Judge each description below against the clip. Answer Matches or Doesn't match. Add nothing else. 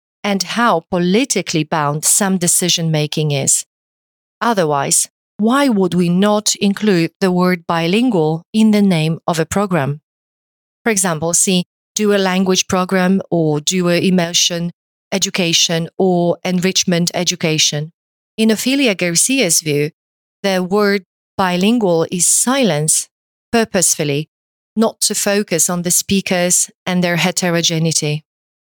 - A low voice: Doesn't match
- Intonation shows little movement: Doesn't match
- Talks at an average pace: Matches